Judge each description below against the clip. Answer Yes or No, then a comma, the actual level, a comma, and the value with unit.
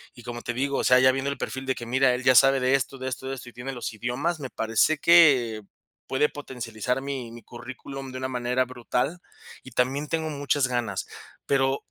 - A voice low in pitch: Yes, low, 130 Hz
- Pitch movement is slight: Yes, narrow, 2.1 semitones